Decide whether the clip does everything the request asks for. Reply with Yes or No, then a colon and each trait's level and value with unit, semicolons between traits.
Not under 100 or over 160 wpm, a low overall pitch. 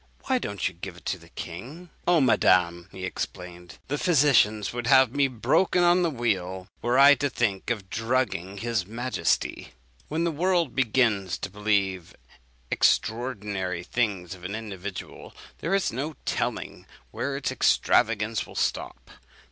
Yes: average, 150 wpm; low, 110 Hz